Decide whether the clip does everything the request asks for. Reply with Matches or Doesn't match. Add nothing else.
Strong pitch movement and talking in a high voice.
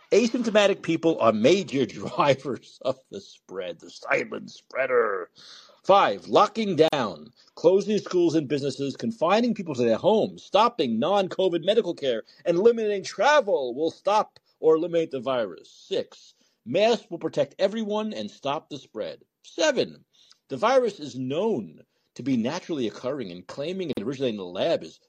Matches